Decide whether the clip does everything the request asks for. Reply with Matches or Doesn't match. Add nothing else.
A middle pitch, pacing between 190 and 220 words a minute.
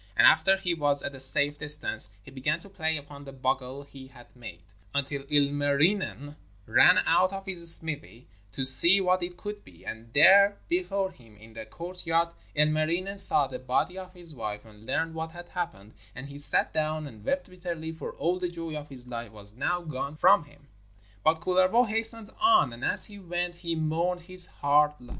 Matches